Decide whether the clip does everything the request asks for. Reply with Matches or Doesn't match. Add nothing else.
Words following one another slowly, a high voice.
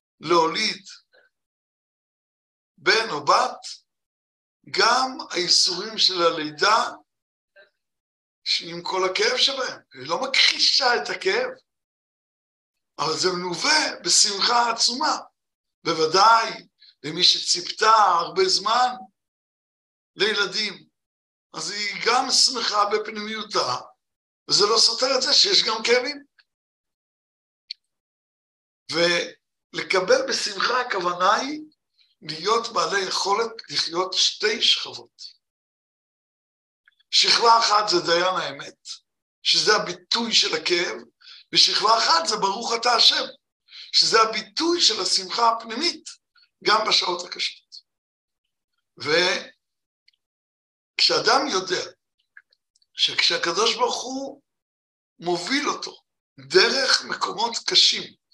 Matches